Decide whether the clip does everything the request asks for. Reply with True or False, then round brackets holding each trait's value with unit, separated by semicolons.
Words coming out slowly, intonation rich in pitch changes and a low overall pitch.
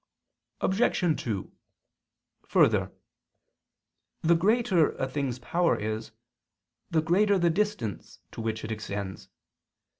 False (100 wpm; 8.6 semitones; 155 Hz)